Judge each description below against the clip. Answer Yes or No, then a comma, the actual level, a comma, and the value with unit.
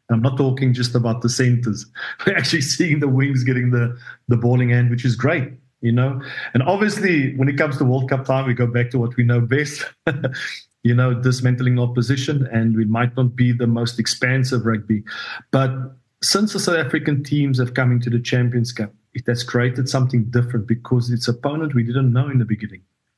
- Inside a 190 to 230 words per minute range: Yes, average, 200 wpm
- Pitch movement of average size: No, narrow, 2.0 semitones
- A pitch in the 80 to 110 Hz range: No, low, 125 Hz